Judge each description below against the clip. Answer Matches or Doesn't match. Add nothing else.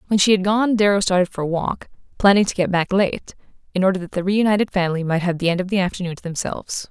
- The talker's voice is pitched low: Doesn't match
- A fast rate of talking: Matches